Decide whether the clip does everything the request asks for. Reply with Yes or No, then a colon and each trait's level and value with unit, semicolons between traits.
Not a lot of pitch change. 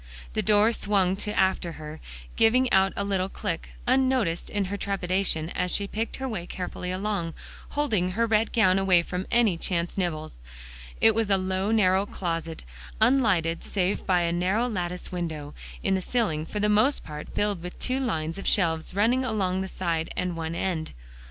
No: average, 3.6 semitones